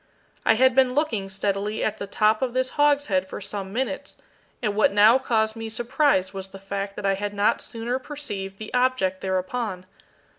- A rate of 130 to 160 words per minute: No, average, 185 wpm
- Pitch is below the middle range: No, high, 215 Hz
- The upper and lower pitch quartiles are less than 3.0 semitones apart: No, average, 4.4 semitones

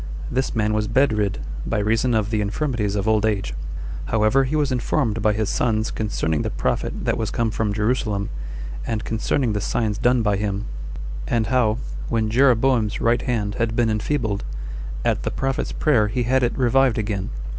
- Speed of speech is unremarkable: Yes, average, 175 wpm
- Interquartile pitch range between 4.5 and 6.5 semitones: No, average, 2.7 semitones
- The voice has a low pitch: Yes, low, 110 Hz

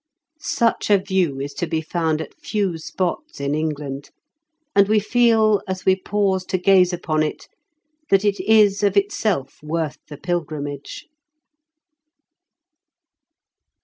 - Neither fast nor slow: No, slow, 130 wpm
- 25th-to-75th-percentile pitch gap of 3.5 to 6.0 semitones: Yes, average, 4.6 semitones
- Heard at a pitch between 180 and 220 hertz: Yes, medium, 185 Hz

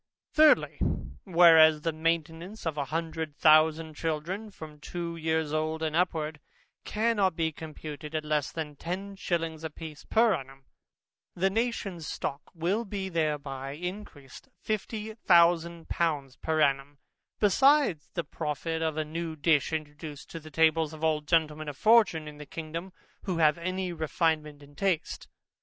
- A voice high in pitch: No, medium, 160 Hz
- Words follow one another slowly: No, average, 150 wpm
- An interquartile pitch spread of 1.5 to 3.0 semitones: Yes, narrow, 2.5 semitones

